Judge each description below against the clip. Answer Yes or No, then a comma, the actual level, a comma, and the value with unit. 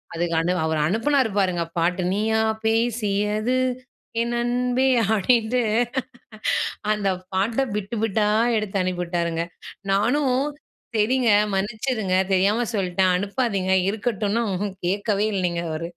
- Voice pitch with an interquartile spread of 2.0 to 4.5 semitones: Yes, average, 3.9 semitones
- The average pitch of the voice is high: Yes, high, 205 Hz